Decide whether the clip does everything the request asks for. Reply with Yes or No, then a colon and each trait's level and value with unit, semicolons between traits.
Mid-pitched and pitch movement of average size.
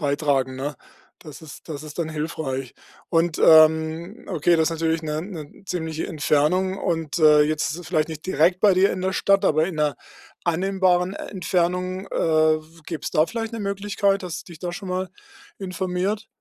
Yes: medium, 165 Hz; average, 3.1 semitones